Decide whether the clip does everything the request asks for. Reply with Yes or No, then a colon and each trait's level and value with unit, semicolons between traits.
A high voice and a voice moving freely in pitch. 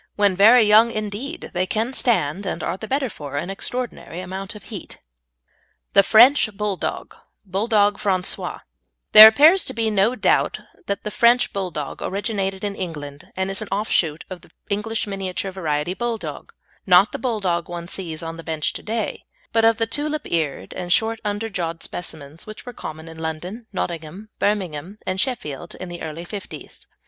No: high, 195 Hz; average, 4.3 semitones